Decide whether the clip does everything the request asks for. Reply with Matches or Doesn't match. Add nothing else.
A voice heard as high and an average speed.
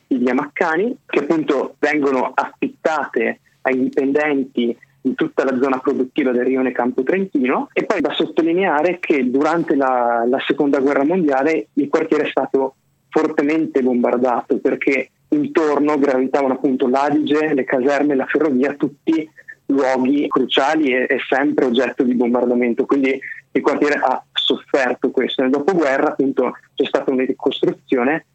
Doesn't match